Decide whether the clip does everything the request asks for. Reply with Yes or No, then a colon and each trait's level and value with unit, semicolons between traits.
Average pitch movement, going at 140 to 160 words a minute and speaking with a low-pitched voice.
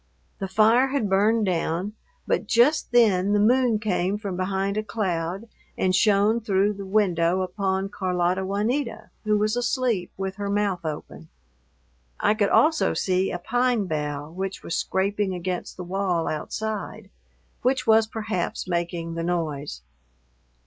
No: average, 3.2 semitones; average, 145 wpm; high, 195 Hz